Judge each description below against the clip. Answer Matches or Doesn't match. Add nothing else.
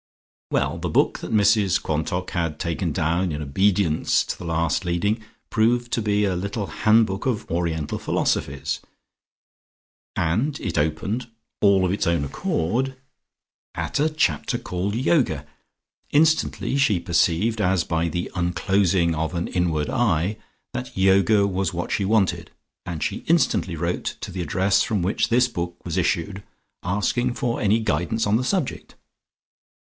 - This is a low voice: Matches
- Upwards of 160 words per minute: Doesn't match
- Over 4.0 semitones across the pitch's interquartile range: Matches